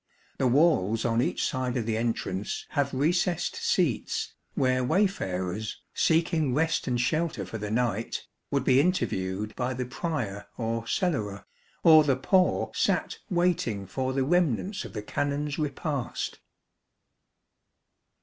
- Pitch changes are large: Yes, wide, 5.8 semitones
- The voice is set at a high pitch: No, low, 130 Hz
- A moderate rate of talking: No, slow, 130 wpm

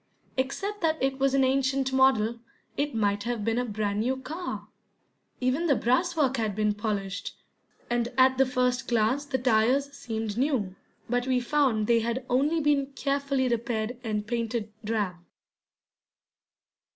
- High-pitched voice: Yes, very high, 250 Hz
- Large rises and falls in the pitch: No, average, 3.6 semitones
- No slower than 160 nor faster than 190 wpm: No, average, 150 wpm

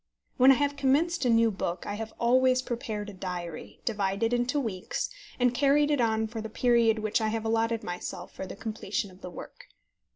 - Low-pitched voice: No, high, 225 Hz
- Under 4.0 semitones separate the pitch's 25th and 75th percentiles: Yes, average, 3.5 semitones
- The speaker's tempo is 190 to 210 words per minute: Yes, average, 200 wpm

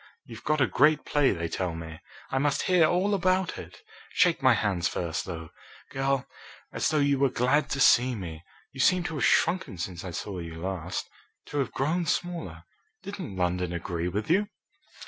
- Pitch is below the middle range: Yes, low, 130 Hz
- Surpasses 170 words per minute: Yes, average, 185 wpm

